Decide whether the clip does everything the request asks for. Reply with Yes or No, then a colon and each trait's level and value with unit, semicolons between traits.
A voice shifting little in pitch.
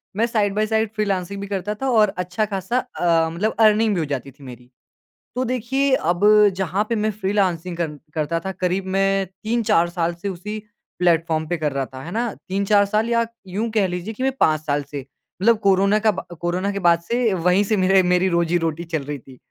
No: average, 4.1 semitones